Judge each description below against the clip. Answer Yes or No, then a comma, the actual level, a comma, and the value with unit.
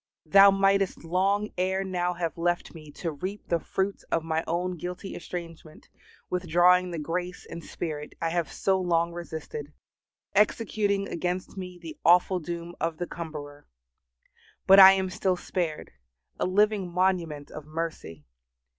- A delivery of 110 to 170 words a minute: Yes, average, 145 wpm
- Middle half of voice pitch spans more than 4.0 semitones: No, narrow, 2.4 semitones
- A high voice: No, medium, 175 Hz